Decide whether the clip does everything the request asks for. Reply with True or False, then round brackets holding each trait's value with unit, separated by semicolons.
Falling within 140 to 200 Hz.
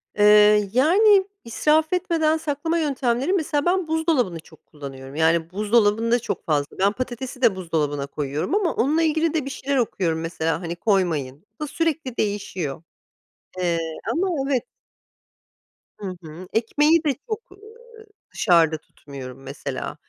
False (230 Hz)